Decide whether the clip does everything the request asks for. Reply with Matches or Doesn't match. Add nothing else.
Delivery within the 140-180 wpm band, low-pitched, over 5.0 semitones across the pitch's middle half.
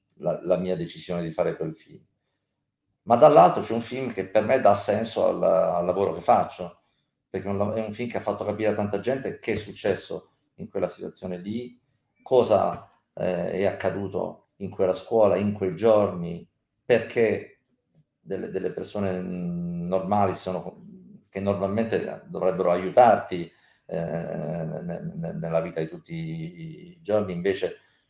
Matches